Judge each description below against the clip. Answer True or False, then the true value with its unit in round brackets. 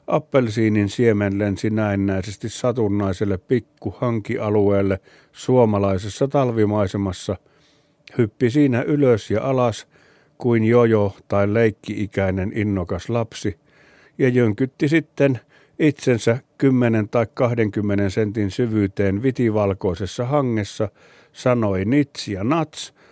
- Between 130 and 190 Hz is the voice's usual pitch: False (115 Hz)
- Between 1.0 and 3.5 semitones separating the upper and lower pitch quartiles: False (4.2 semitones)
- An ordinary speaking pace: False (90 wpm)